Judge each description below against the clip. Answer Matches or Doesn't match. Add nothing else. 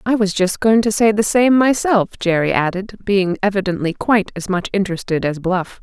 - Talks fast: Doesn't match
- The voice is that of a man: Doesn't match